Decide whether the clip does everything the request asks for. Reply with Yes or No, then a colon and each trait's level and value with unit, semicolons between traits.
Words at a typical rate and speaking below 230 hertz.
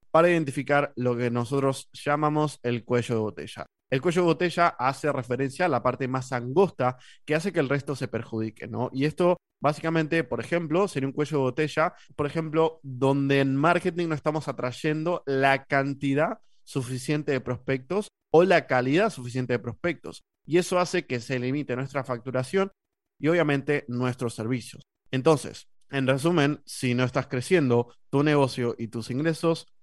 Yes: average, 165 wpm; medium, 140 Hz